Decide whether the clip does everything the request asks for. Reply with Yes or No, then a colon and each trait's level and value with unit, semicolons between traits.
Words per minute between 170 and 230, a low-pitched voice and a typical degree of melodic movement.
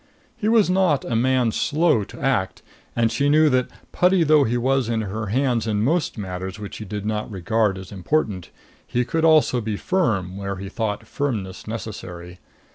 No: average, 180 wpm; low, 115 Hz; wide, 6.0 semitones